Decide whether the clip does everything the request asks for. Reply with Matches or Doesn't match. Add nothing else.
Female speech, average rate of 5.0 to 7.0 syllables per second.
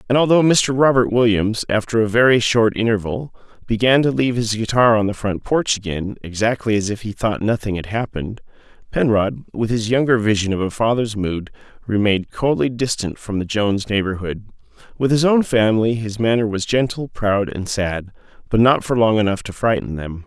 Doesn't match